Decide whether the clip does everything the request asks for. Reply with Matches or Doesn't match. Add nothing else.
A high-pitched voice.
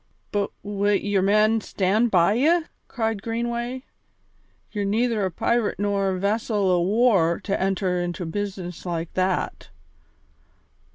Matches